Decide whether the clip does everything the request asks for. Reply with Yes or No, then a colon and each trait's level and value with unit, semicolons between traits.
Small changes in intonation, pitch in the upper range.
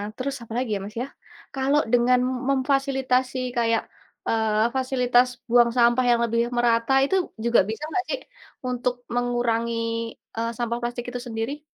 Yes: narrow, 2.0 semitones; high, 245 Hz